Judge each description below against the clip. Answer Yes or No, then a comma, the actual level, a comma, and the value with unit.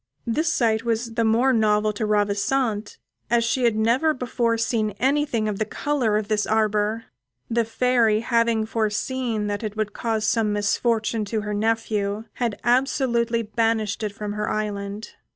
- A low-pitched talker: No, high, 220 Hz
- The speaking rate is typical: Yes, average, 160 wpm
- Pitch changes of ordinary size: No, narrow, 1.8 semitones